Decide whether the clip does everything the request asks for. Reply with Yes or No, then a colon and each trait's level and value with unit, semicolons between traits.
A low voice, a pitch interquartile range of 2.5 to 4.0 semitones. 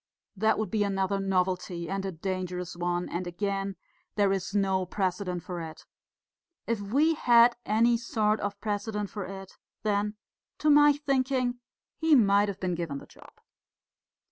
No: high, 200 Hz; average, 3.1 semitones